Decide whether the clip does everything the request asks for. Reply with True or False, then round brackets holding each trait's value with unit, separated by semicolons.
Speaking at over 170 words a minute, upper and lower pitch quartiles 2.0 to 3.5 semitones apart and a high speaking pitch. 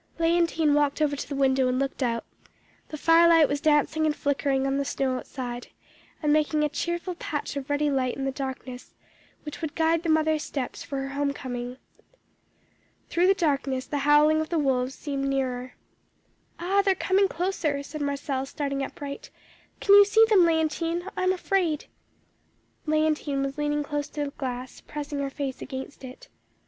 True (180 wpm; 2.8 semitones; 290 Hz)